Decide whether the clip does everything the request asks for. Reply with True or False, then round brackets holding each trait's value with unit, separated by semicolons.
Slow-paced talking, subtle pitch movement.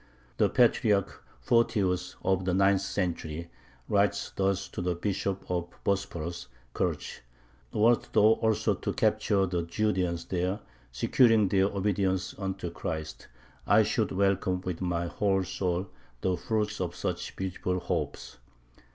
True (130 wpm; 2.1 semitones)